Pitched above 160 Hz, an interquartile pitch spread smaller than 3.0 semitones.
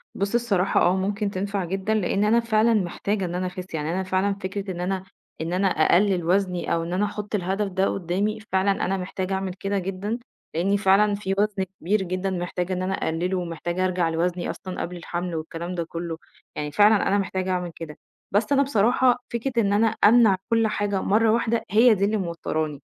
Yes: high, 190 Hz; narrow, 2.6 semitones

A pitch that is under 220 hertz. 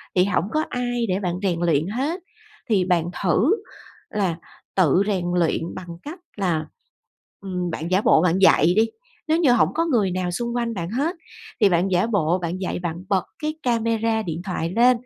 Yes: high, 190 Hz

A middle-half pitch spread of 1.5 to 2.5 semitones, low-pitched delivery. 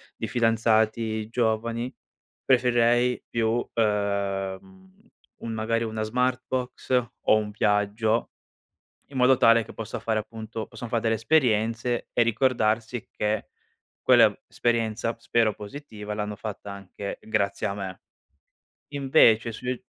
Yes: narrow, 2.1 semitones; low, 115 Hz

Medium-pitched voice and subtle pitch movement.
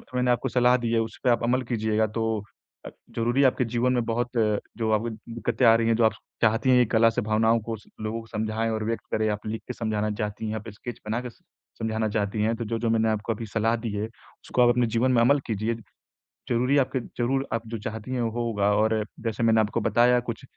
No: low, 115 Hz; narrow, 1.6 semitones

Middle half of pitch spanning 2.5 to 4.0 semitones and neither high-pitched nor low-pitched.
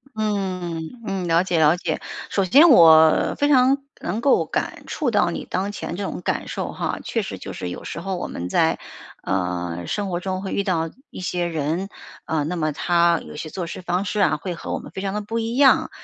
Yes: average, 3.7 semitones; medium, 180 Hz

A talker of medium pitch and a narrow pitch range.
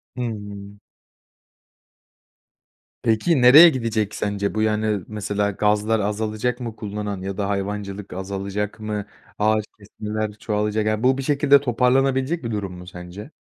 No: low, 105 Hz; narrow, 2.2 semitones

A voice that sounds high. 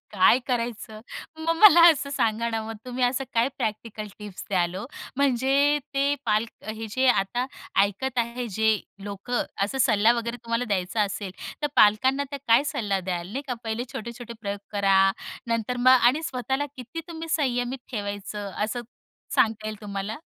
Yes: high, 230 Hz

